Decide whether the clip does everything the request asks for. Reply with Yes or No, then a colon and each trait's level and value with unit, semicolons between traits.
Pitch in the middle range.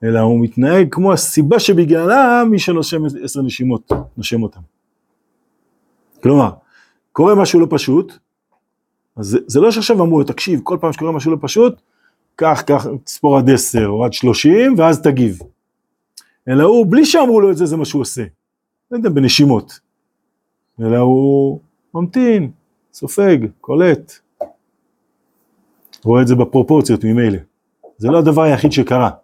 Yes: medium, 145 Hz